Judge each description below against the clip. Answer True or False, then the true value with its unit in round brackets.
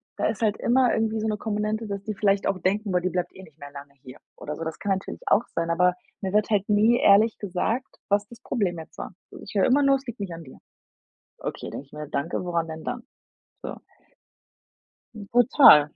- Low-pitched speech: False (200 Hz)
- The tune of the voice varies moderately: True (4.7 semitones)